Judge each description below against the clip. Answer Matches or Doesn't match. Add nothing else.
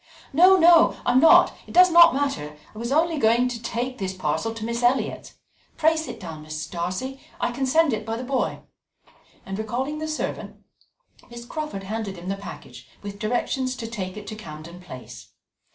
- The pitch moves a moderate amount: Doesn't match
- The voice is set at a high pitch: Matches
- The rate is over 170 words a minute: Matches